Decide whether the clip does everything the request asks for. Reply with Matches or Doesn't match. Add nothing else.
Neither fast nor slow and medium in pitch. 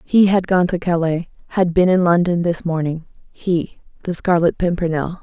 Matches